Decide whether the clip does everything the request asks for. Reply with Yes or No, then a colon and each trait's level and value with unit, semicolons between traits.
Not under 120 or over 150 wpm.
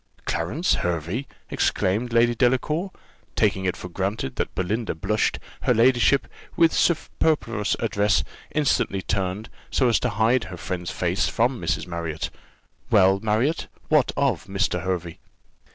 Yes: slow, 135 wpm